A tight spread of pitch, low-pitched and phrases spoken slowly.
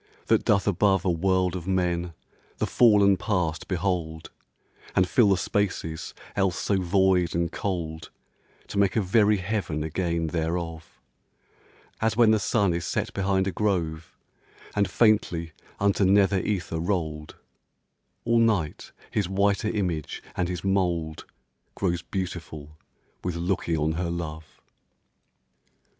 No: average, 3.1 semitones; very low, 90 Hz; slow, 130 wpm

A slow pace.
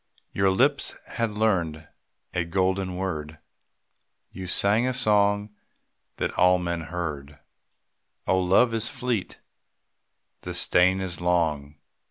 Yes: slow, 115 wpm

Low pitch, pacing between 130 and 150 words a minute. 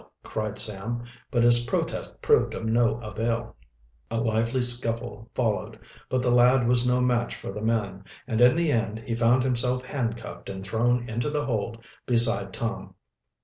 No: low, 115 Hz; average, 165 wpm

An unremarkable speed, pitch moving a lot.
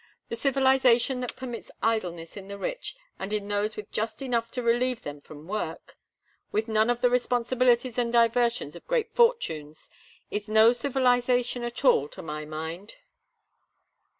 No: average, 155 wpm; average, 3.6 semitones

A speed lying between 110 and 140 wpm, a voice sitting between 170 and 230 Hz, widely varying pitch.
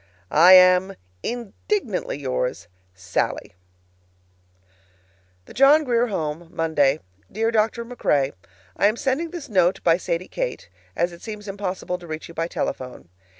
Yes: slow, 135 wpm; medium, 185 Hz; wide, 6.1 semitones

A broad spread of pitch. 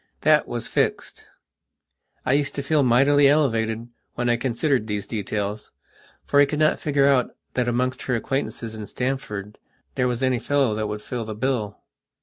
No: average, 4.0 semitones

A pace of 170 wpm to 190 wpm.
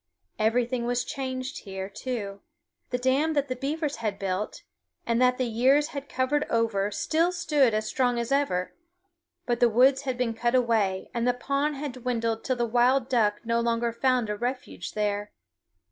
Yes: average, 175 wpm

